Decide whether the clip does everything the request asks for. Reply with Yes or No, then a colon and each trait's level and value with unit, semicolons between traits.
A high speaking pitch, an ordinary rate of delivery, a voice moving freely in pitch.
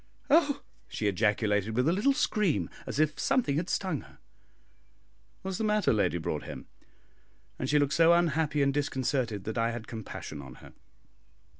No: medium, 140 Hz; average, 165 wpm; wide, 7.8 semitones